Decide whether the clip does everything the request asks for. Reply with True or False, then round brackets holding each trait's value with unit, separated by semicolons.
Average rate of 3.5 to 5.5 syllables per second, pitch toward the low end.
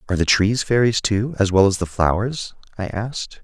True (5.4 syllables/s; 105 Hz)